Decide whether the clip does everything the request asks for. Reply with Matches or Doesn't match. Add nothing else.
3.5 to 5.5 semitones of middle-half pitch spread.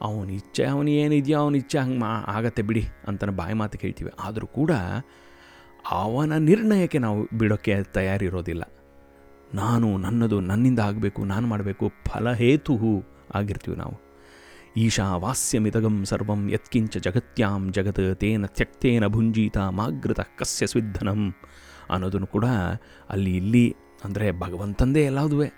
Matches